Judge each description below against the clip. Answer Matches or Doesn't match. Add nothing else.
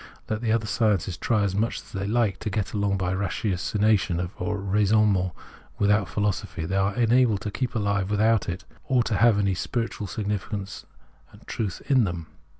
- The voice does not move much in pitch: Matches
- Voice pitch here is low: Matches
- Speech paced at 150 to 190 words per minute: Matches